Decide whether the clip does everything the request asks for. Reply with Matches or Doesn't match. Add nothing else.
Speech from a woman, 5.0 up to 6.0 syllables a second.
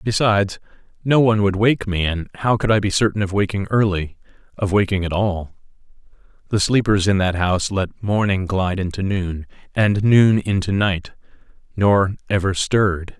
Doesn't match